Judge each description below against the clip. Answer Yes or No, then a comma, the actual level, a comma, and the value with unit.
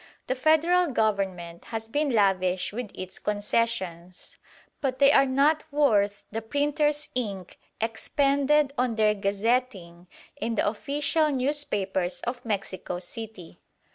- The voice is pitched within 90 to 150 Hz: No, high, 225 Hz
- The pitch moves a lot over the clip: Yes, wide, 6.2 semitones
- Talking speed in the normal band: No, slow, 120 wpm